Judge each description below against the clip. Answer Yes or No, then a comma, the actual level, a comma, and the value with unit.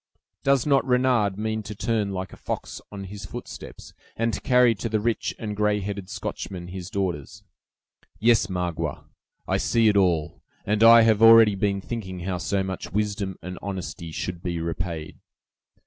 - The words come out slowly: No, average, 170 wpm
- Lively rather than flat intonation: No, average, 3.2 semitones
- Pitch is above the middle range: No, low, 100 Hz